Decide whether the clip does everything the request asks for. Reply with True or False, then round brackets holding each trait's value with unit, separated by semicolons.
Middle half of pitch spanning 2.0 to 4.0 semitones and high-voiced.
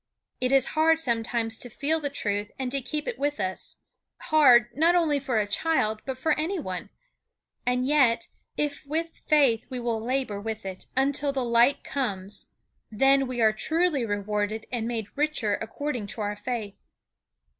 False (4.9 semitones; 250 Hz)